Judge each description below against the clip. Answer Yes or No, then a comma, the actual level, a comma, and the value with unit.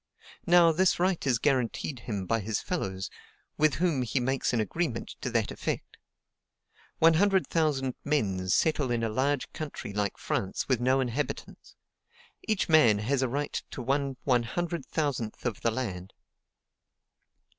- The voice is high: No, low, 130 Hz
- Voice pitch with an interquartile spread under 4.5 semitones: No, average, 5.3 semitones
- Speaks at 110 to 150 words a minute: Yes, average, 145 wpm